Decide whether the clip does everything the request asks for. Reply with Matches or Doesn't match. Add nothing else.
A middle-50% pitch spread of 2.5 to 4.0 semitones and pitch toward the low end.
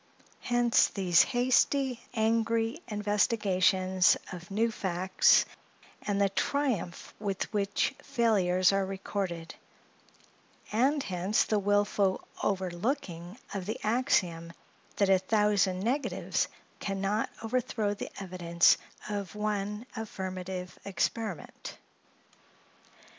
Doesn't match